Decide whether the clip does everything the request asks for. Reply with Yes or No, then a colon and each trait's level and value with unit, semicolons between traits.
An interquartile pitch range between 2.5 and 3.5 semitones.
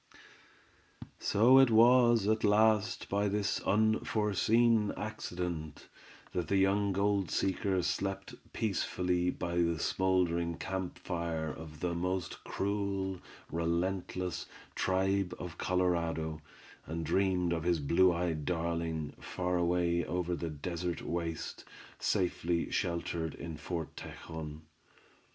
Yes: average, 2.8 semitones